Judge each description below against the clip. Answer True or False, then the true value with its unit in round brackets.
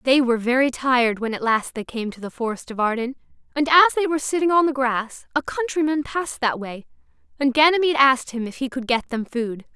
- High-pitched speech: True (260 Hz)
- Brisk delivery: True (230 wpm)